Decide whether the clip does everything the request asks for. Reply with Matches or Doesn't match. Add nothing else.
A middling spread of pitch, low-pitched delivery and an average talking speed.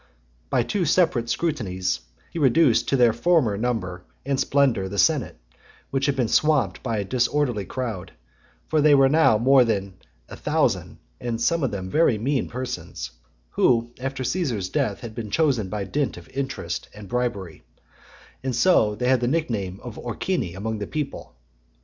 Matches